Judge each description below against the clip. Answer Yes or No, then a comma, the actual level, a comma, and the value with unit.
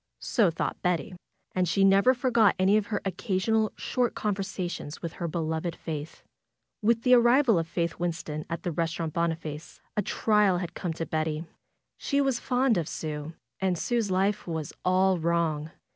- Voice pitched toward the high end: No, medium, 180 Hz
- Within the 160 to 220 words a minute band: Yes, average, 165 wpm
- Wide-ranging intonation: No, average, 4.3 semitones